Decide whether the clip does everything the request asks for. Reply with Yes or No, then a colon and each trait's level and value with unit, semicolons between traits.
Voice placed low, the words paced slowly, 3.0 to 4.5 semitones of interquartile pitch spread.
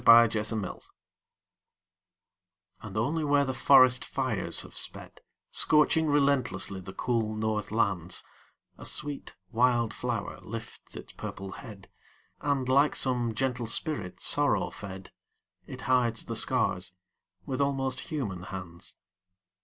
No: low, 120 Hz; slow, 120 wpm; average, 4.9 semitones